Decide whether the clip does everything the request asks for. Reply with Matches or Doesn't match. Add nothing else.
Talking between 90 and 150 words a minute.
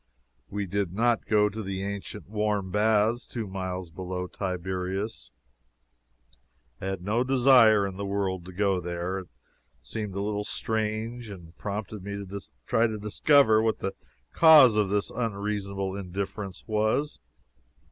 Matches